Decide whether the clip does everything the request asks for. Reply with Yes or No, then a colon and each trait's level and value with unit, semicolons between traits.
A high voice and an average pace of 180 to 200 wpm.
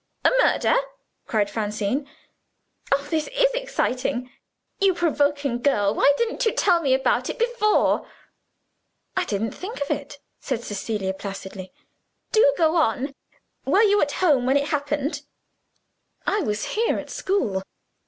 No: very high, 285 Hz; average, 140 wpm